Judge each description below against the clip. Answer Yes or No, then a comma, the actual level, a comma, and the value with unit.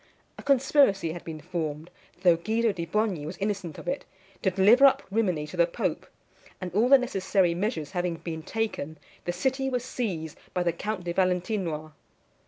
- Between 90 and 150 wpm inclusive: No, average, 180 wpm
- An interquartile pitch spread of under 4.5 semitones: No, average, 4.8 semitones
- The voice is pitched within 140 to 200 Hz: Yes, medium, 185 Hz